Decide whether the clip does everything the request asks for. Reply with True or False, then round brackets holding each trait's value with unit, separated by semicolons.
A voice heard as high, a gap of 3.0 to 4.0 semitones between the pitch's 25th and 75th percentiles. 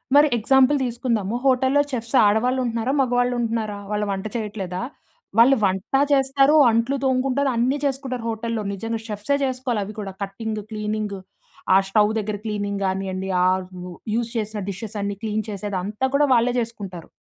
True (225 Hz; 3.6 semitones)